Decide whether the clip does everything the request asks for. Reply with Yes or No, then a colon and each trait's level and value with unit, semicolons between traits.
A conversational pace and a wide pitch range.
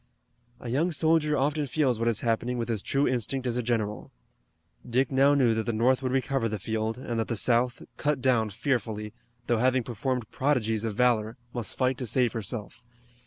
No: average, 195 wpm; average, 2.8 semitones